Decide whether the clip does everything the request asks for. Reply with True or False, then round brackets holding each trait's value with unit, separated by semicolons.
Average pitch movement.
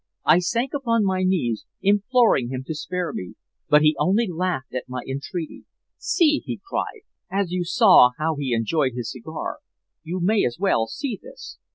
False (7.2 semitones)